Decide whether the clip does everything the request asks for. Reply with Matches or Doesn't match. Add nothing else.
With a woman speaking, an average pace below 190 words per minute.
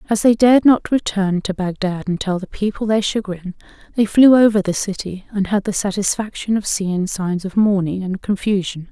Doesn't match